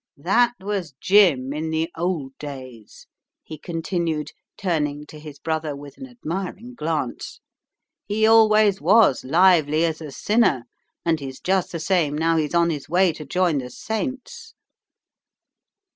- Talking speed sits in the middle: Yes, average, 145 wpm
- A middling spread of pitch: Yes, average, 4.7 semitones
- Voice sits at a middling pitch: Yes, medium, 165 Hz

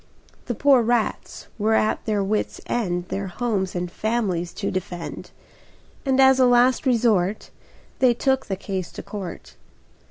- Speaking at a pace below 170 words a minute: Yes, average, 150 wpm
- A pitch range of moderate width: Yes, average, 4.5 semitones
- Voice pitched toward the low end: No, high, 215 Hz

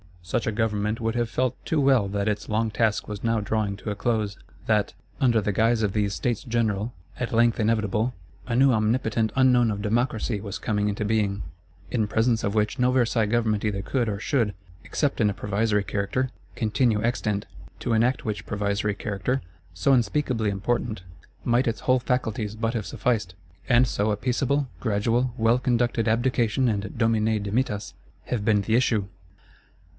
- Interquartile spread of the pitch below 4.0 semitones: Yes, narrow, 2.6 semitones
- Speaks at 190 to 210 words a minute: No, average, 175 wpm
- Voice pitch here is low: Yes, low, 110 Hz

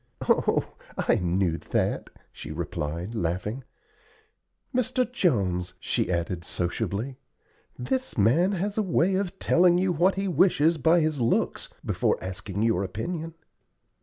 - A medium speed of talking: No, slow, 130 wpm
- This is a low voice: Yes, low, 130 Hz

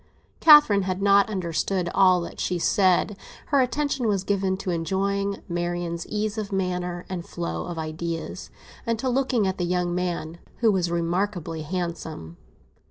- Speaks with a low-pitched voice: No, medium, 185 Hz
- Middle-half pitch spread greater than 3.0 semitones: No, average, 2.7 semitones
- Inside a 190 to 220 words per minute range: No, average, 155 wpm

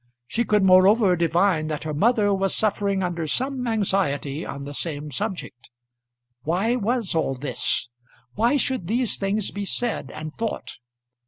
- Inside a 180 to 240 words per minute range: No, average, 150 wpm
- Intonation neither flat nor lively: No, wide, 5.8 semitones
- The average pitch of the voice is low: No, high, 195 Hz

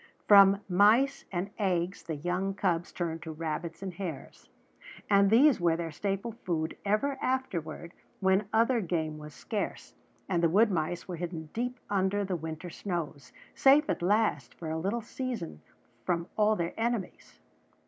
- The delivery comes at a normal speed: Yes, average, 160 wpm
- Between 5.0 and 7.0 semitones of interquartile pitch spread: No, average, 4.2 semitones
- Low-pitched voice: No, medium, 185 Hz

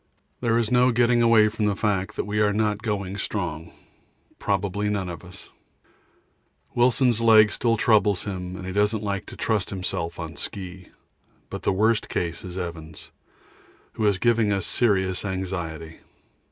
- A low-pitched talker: Yes, low, 100 Hz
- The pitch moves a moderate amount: Yes, average, 3.1 semitones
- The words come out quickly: No, average, 160 wpm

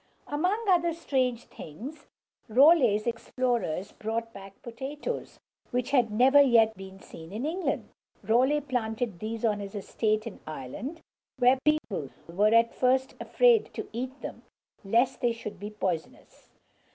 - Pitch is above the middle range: Yes, high, 235 Hz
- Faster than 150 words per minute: No, average, 140 wpm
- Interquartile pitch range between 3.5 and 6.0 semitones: Yes, average, 4.1 semitones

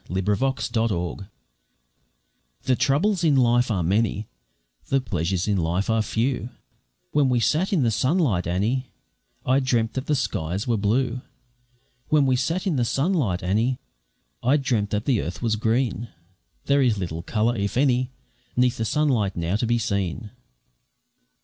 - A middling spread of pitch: Yes, average, 4.7 semitones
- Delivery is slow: No, average, 155 wpm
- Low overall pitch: Yes, low, 115 Hz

